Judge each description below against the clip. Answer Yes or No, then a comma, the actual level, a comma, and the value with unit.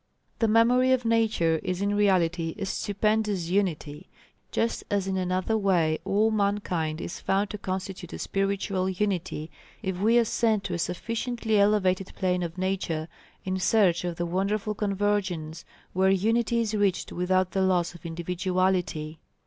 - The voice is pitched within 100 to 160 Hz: No, high, 190 Hz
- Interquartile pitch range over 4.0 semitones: No, average, 2.9 semitones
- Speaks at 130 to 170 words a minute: Yes, average, 150 wpm